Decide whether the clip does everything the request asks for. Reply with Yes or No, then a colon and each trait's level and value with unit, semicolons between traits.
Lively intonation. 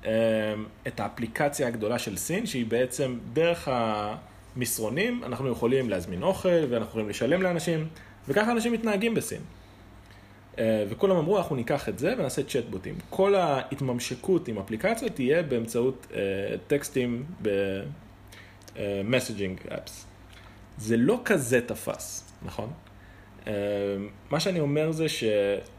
Yes: wide, 6.8 semitones